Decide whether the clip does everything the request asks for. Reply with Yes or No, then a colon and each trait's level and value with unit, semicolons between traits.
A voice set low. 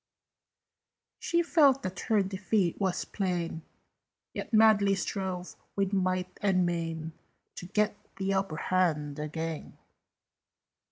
No: medium, 185 Hz